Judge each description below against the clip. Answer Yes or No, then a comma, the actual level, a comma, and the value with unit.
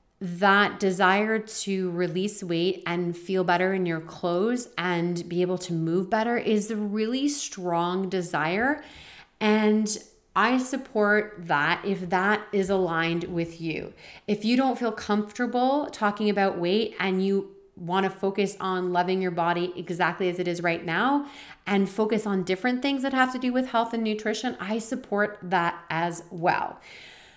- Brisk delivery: No, average, 160 wpm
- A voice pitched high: Yes, high, 195 Hz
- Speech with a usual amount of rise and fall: Yes, average, 3.5 semitones